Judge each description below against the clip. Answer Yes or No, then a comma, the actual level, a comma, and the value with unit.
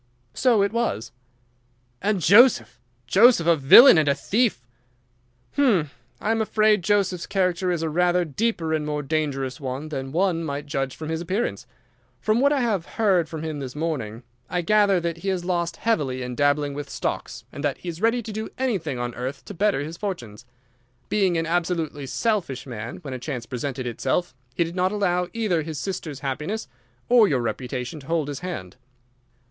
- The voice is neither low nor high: Yes, medium, 165 Hz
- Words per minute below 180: No, average, 185 wpm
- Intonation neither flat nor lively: No, wide, 6.1 semitones